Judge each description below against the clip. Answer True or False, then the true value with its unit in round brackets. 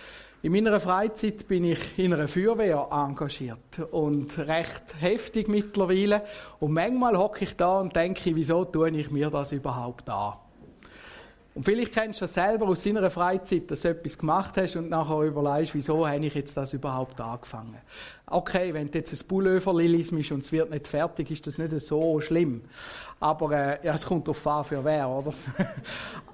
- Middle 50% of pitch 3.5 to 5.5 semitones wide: True (4.1 semitones)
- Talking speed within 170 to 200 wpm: True (175 wpm)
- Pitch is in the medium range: True (160 Hz)